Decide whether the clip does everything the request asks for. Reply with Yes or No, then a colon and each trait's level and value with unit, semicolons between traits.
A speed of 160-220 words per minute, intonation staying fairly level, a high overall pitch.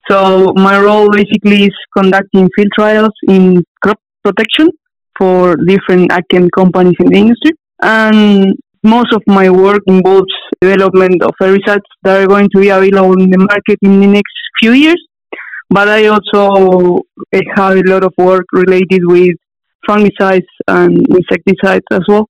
No: average, 150 wpm; narrow, 1.8 semitones; high, 195 Hz